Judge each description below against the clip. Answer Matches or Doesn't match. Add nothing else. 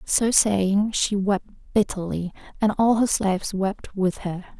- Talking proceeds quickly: Doesn't match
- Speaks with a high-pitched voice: Matches